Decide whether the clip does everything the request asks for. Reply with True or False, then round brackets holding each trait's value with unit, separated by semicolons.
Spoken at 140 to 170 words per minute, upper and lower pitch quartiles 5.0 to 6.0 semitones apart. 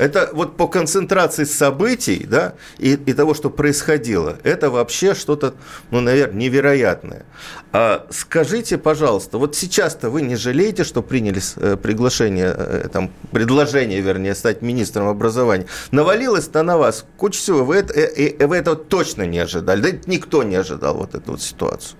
True (155 wpm; 5.5 semitones)